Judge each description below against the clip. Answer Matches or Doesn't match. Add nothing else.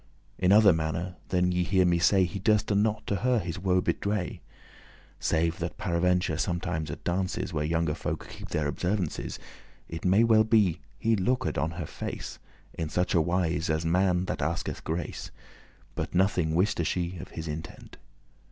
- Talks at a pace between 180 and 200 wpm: Doesn't match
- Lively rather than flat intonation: Doesn't match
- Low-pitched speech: Matches